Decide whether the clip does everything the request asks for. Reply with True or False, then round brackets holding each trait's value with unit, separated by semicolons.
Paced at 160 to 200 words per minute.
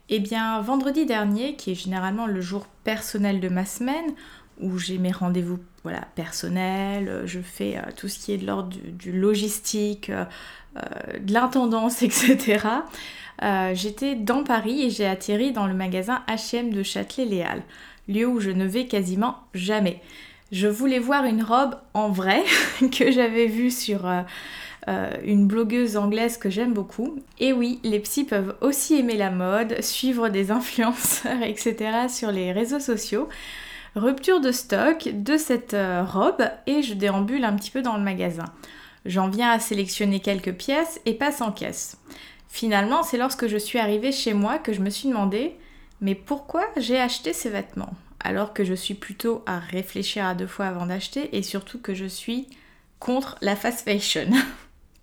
True (170 wpm)